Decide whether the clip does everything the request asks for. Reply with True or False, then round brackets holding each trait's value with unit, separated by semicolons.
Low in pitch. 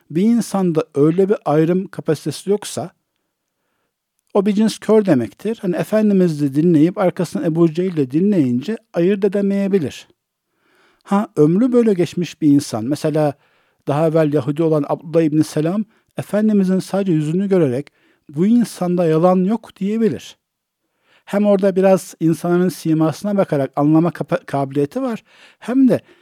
False (180 Hz)